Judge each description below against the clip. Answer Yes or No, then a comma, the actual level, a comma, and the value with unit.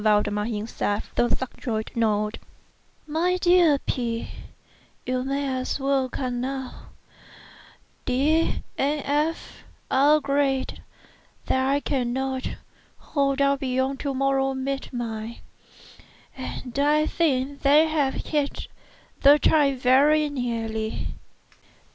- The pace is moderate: No, slow, 105 wpm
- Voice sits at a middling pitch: No, very high, 270 Hz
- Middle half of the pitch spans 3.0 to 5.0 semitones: No, narrow, 2.6 semitones